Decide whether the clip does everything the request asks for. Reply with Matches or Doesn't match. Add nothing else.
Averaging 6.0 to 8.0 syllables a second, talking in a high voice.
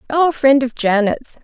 Doesn't match